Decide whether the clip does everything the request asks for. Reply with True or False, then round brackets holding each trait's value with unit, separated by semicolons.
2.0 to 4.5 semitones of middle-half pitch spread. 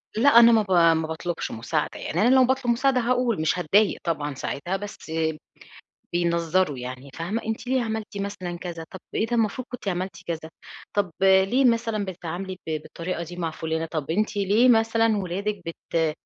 False (5.0 semitones)